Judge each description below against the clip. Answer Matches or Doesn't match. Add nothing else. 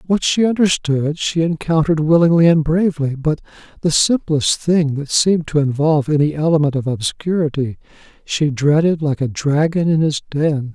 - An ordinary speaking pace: Matches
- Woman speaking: Doesn't match